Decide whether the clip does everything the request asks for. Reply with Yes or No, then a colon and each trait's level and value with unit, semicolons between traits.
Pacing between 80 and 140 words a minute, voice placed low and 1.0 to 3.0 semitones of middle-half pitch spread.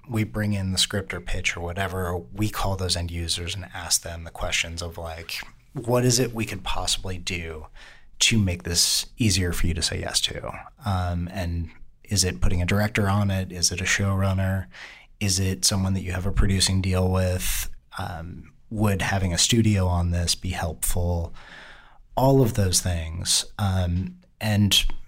No: average, 180 wpm; very low, 95 Hz; narrow, 2.5 semitones